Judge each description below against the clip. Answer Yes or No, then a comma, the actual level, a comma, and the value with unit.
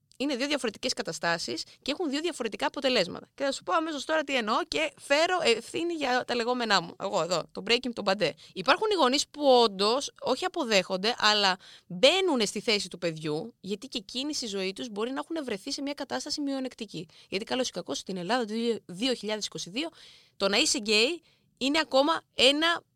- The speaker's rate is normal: No, fast, 190 wpm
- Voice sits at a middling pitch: No, very high, 250 Hz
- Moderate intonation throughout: No, wide, 5.9 semitones